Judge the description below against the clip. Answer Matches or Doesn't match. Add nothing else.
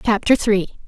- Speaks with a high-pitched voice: Matches